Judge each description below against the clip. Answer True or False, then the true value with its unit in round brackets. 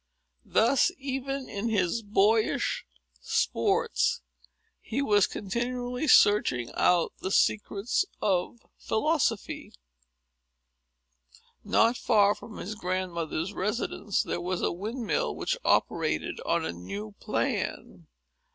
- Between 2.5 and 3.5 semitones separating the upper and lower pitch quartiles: False (4.8 semitones)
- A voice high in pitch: True (210 Hz)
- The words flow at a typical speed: False (100 wpm)